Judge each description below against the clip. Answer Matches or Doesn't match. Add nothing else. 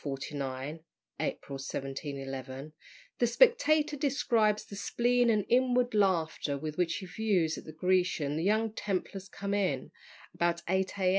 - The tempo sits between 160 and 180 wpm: Doesn't match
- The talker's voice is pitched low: Doesn't match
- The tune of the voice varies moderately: Doesn't match